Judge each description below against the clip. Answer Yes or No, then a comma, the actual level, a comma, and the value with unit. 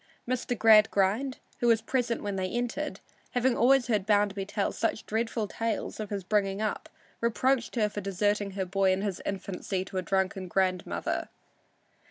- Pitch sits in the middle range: No, high, 210 Hz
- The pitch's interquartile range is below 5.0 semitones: Yes, average, 3.2 semitones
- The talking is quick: No, average, 165 wpm